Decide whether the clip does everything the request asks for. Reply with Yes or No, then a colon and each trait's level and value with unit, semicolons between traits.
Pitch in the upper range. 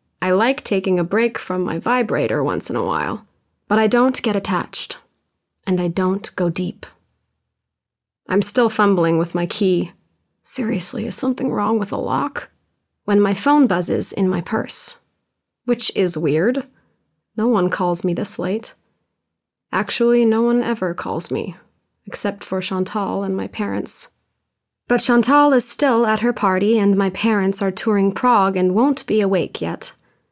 Yes: high, 205 Hz